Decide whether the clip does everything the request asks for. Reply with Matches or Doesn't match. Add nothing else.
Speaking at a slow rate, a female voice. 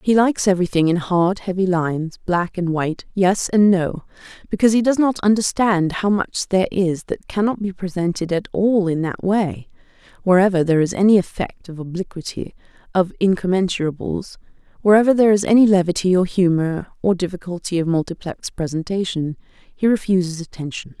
Doesn't match